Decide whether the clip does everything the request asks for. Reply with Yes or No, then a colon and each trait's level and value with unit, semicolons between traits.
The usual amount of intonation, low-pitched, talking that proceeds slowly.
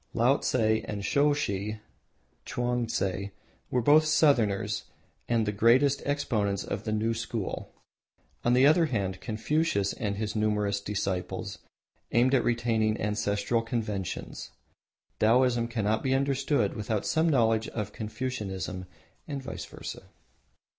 Yes: average, 3.7 semitones; low, 115 Hz; slow, 120 wpm